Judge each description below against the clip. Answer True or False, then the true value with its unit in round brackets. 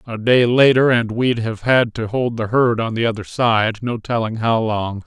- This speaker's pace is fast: True (225 wpm)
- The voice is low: True (115 Hz)